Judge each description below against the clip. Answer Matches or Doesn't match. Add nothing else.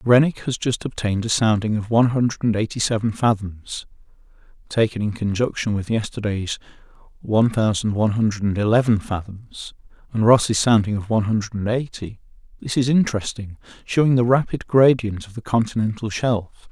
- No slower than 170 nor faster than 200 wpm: Doesn't match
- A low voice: Matches